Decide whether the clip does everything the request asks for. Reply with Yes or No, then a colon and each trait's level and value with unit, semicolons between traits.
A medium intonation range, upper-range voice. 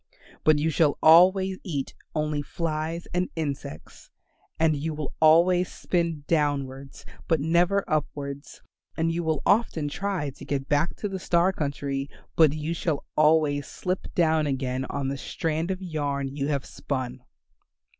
No: average, 3.1 semitones; medium, 155 Hz